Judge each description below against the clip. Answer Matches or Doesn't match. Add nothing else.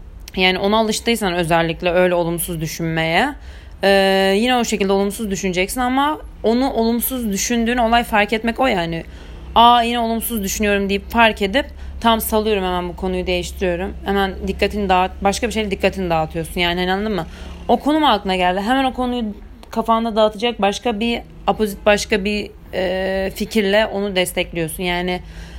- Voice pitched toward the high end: Matches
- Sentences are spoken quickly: Matches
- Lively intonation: Doesn't match